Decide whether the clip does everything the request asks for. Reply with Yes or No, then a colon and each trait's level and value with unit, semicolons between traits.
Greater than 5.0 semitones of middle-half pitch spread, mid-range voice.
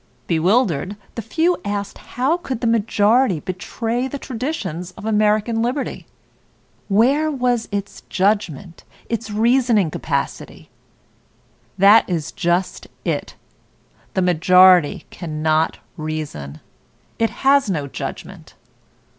No: wide, 5.6 semitones; high, 205 Hz